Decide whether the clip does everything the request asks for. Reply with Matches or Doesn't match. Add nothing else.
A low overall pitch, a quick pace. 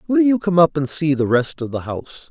Doesn't match